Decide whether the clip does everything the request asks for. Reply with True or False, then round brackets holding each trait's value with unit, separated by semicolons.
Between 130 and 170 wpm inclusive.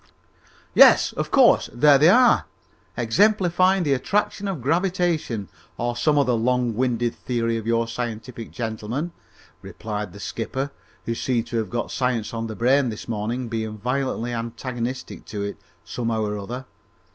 True (150 wpm)